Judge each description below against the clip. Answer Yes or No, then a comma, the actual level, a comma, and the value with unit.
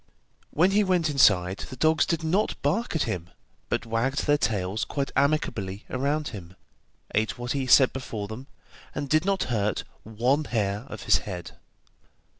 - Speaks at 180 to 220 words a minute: No, average, 165 wpm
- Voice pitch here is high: No, low, 130 Hz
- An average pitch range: No, wide, 6.5 semitones